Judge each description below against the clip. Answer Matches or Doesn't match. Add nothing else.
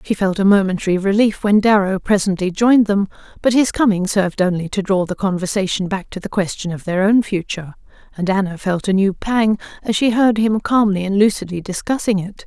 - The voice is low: Doesn't match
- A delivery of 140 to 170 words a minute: Doesn't match